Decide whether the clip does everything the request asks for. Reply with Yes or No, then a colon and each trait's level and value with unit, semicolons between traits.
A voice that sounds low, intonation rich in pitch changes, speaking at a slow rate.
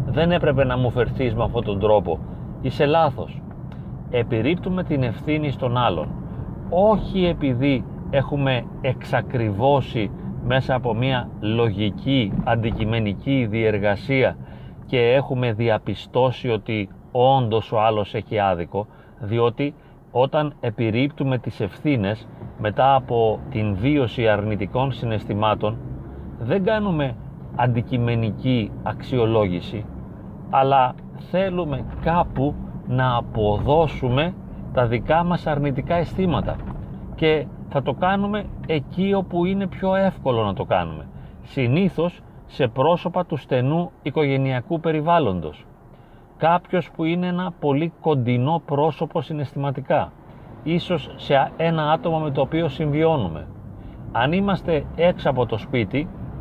Yes: low, 130 Hz; wide, 5.8 semitones; slow, 105 wpm